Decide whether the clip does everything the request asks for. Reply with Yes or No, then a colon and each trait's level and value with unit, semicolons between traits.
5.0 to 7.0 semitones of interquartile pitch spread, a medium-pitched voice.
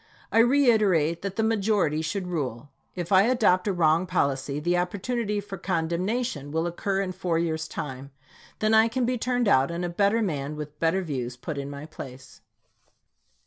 Yes: wide, 5.4 semitones; medium, 175 Hz